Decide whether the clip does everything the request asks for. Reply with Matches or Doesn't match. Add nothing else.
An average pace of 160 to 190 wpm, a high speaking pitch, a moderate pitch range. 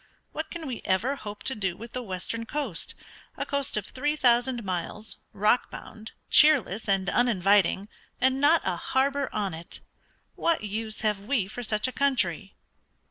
Matches